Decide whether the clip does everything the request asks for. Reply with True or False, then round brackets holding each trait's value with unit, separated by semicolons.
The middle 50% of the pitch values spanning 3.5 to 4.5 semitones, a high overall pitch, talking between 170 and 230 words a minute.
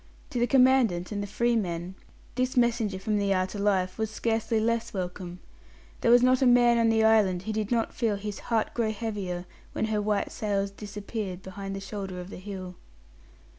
False (3.1 semitones; 210 Hz; 195 wpm)